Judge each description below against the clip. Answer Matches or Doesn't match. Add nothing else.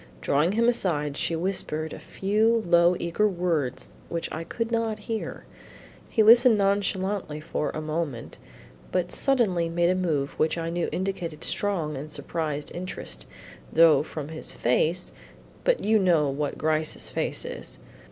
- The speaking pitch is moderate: Matches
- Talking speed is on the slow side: Doesn't match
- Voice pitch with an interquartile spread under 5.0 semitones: Matches